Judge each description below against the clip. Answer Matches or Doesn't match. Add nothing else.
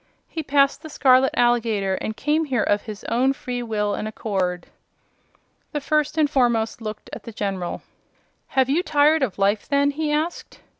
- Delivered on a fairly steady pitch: Doesn't match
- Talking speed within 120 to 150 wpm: Doesn't match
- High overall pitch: Matches